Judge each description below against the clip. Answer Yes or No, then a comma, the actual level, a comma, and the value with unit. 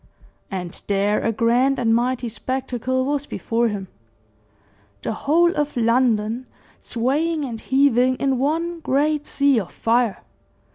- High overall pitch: Yes, very high, 255 Hz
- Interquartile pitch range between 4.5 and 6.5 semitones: No, average, 3.6 semitones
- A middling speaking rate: No, slow, 130 wpm